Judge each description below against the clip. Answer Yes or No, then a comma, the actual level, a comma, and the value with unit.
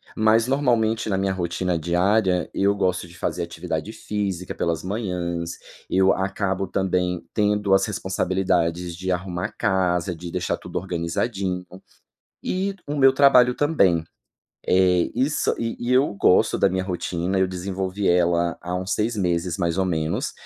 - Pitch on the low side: Yes, very low, 95 Hz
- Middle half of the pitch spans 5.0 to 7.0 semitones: No, average, 2.9 semitones